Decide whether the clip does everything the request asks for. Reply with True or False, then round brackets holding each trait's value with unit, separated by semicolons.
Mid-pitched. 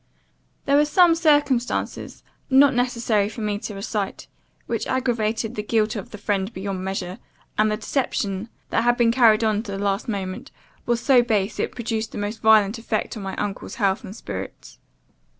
False (220 Hz)